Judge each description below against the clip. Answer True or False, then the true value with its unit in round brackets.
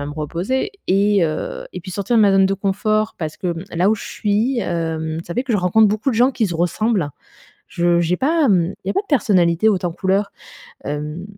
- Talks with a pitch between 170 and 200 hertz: True (190 Hz)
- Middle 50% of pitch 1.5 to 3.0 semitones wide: False (4.0 semitones)